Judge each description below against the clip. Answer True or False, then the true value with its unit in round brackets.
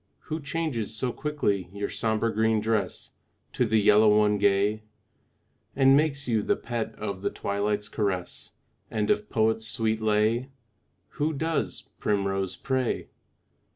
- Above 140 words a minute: False (135 wpm)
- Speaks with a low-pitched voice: True (110 Hz)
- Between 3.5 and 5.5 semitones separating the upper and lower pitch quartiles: False (3.0 semitones)